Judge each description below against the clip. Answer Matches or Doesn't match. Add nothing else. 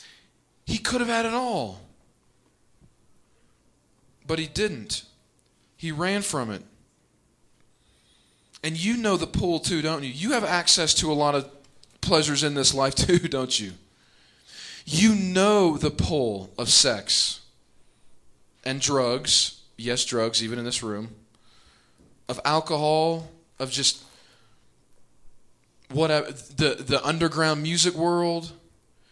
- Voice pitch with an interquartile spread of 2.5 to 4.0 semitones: Doesn't match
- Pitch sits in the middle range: Matches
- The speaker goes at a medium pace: Doesn't match